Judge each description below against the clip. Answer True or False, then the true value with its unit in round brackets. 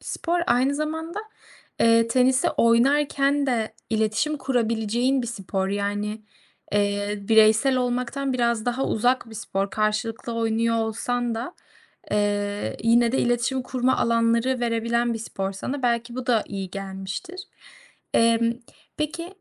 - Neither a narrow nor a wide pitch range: True (3.0 semitones)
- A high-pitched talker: True (235 Hz)